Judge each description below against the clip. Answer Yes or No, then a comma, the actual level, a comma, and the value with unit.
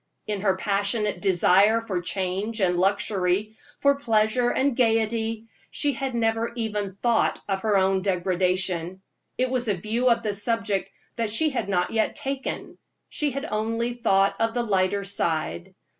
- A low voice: No, high, 215 Hz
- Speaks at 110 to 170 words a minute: Yes, average, 160 wpm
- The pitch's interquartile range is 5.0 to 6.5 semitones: No, average, 3.3 semitones